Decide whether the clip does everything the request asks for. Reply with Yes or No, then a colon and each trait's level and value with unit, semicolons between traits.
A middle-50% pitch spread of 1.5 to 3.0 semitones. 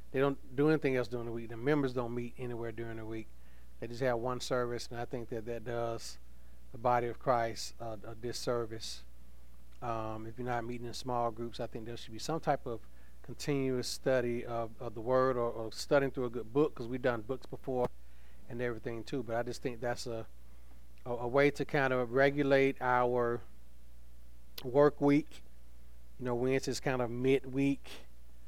Yes: average, 2.7 semitones